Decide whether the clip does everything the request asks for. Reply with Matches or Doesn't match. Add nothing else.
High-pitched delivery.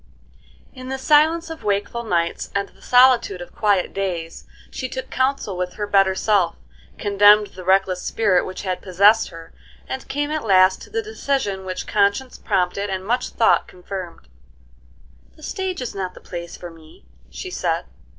Matches